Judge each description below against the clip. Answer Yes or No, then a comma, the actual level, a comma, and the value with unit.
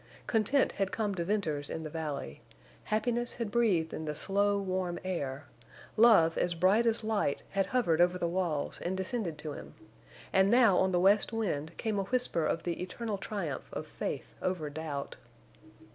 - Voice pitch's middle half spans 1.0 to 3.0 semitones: No, average, 4.8 semitones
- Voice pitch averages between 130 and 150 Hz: No, medium, 185 Hz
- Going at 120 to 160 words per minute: No, average, 175 wpm